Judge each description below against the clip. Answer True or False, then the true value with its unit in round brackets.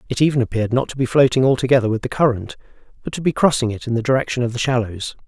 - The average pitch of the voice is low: True (125 Hz)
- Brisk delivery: True (250 wpm)